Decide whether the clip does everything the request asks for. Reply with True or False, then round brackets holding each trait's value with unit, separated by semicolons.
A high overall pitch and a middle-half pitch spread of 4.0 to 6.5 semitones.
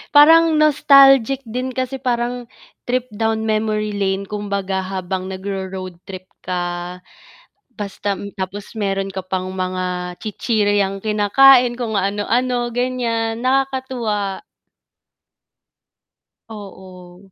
True (210 Hz; 4.4 semitones)